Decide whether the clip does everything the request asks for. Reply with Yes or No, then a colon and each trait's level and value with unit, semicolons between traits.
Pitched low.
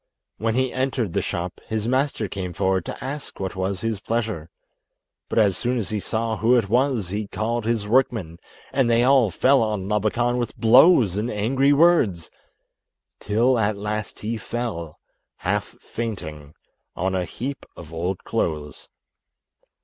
Yes: low, 110 Hz